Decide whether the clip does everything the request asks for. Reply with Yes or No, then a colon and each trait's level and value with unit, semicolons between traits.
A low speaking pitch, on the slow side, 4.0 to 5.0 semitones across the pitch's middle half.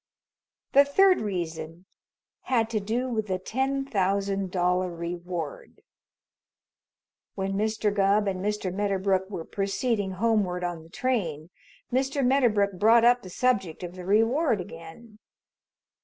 No: high, 200 Hz; slow, 125 wpm; average, 4.3 semitones